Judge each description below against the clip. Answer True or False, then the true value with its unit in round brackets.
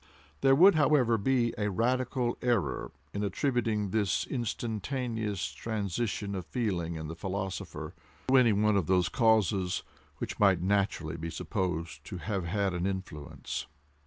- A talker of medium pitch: False (100 Hz)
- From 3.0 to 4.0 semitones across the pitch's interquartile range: False (4.5 semitones)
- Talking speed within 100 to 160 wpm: True (140 wpm)